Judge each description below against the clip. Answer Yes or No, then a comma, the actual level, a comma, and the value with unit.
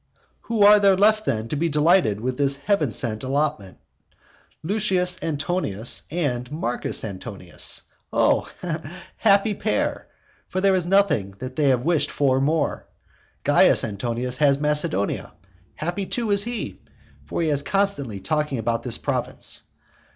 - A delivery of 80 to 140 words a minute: Yes, slow, 135 wpm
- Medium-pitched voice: Yes, medium, 150 Hz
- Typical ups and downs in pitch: No, wide, 7.3 semitones